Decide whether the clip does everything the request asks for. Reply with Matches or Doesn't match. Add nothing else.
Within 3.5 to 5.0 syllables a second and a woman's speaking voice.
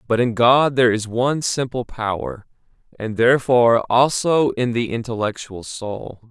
Doesn't match